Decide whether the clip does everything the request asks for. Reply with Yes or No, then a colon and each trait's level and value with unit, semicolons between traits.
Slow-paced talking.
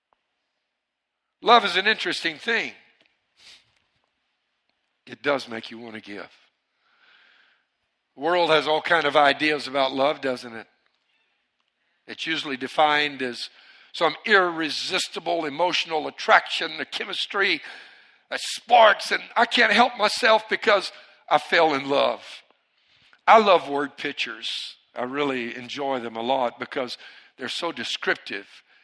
Yes: slow, 125 wpm